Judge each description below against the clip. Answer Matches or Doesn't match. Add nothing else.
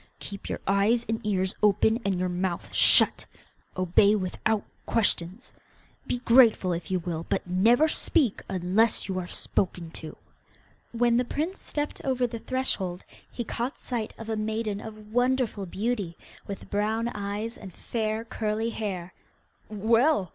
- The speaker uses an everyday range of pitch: Matches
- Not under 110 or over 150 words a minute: Matches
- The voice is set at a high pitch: Matches